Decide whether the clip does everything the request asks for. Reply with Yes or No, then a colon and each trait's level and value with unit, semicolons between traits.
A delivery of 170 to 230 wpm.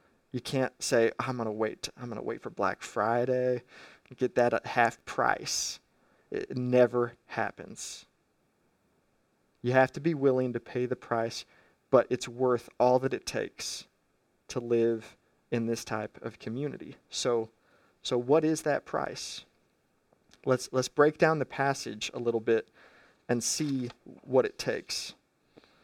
No: average, 155 wpm